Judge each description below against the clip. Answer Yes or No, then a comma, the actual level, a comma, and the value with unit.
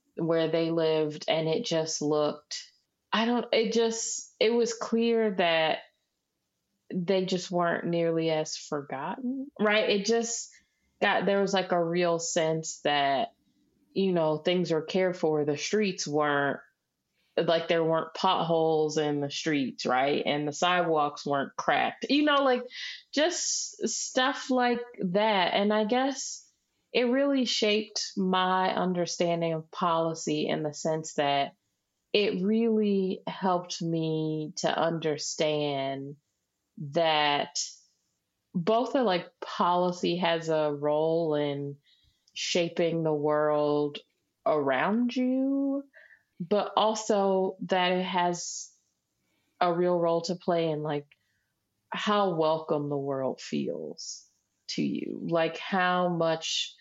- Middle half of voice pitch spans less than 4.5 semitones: No, wide, 5.6 semitones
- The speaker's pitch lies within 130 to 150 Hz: No, medium, 175 Hz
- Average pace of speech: No, slow, 125 wpm